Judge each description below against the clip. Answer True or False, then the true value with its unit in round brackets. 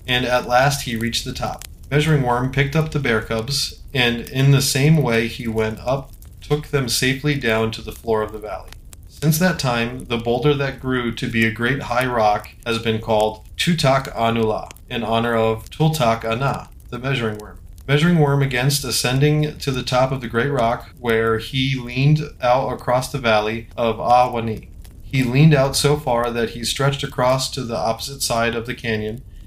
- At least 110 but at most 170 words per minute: False (190 wpm)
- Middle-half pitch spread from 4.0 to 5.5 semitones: False (3.5 semitones)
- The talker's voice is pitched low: True (125 Hz)